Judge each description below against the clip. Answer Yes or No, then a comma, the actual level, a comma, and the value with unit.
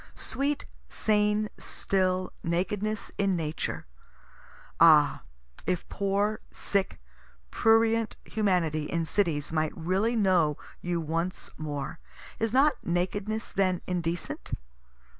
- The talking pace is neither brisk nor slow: No, slow, 100 wpm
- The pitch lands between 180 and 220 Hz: Yes, medium, 185 Hz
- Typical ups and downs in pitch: Yes, average, 4.2 semitones